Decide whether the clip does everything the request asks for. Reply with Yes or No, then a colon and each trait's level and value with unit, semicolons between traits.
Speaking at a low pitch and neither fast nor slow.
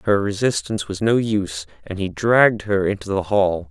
Yes: low, 100 Hz; average, 195 wpm